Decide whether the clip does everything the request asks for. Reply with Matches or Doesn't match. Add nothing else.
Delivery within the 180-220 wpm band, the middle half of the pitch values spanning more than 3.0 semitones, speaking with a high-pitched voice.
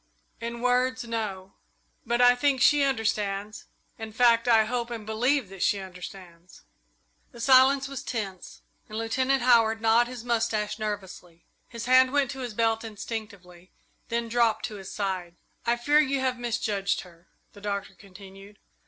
Doesn't match